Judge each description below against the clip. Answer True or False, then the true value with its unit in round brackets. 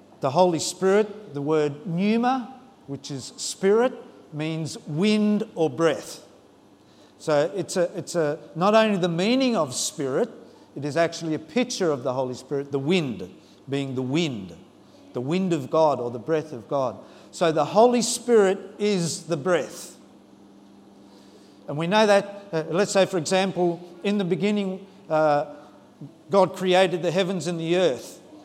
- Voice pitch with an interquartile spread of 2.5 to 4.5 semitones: False (5.3 semitones)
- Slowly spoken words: False (155 wpm)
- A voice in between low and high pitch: True (170 Hz)